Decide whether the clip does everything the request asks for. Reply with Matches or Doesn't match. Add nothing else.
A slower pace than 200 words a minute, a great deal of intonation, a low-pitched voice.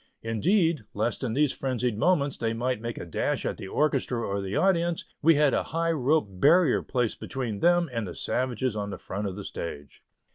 Doesn't match